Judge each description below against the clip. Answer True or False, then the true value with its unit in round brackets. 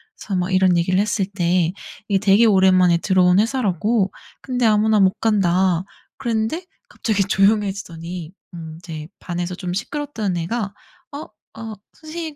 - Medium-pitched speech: False (195 Hz)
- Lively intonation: False (3.5 semitones)